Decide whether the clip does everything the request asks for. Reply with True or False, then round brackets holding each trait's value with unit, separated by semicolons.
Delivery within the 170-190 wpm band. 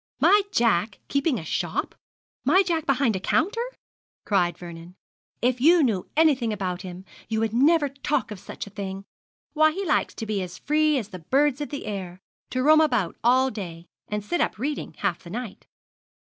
True (185 wpm)